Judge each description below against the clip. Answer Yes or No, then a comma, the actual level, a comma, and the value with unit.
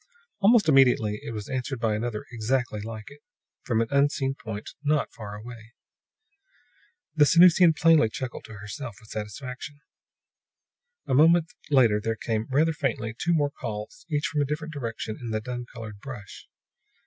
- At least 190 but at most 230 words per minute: No, average, 160 wpm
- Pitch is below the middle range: Yes, low, 125 Hz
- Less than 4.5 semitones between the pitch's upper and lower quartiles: No, average, 5.0 semitones